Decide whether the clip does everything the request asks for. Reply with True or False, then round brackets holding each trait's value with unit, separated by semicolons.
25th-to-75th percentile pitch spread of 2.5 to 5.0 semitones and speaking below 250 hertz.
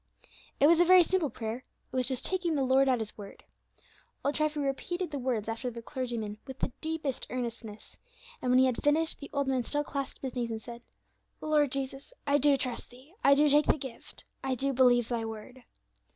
False (3.3 semitones; 265 Hz)